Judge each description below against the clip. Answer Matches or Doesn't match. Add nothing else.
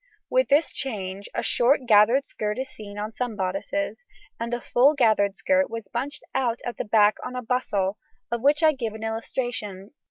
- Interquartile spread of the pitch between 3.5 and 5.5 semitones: Matches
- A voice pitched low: Doesn't match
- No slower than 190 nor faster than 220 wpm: Matches